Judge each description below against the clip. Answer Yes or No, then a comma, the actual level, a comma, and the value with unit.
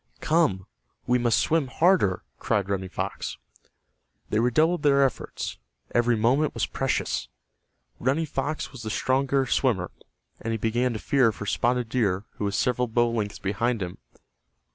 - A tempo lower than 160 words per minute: Yes, average, 150 wpm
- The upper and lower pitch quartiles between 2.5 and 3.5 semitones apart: No, average, 4.2 semitones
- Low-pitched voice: Yes, low, 120 Hz